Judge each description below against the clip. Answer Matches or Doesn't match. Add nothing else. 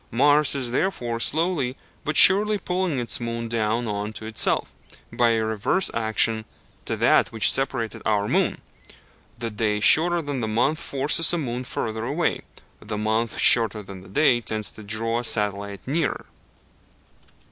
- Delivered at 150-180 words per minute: Matches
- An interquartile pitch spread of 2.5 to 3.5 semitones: Doesn't match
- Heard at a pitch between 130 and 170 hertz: Doesn't match